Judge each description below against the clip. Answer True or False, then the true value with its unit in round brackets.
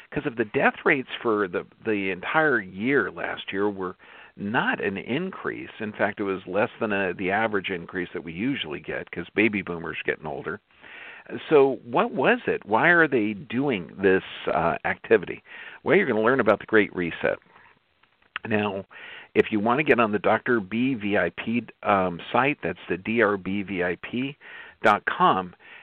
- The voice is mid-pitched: False (100 Hz)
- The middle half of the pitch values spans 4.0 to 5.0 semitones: False (3.2 semitones)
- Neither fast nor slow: True (165 wpm)